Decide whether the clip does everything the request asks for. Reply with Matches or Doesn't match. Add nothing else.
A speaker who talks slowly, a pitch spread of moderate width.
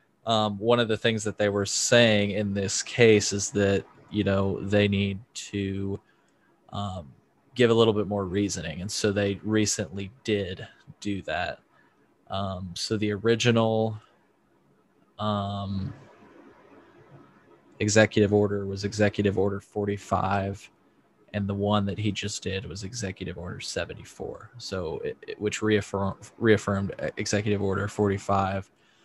Doesn't match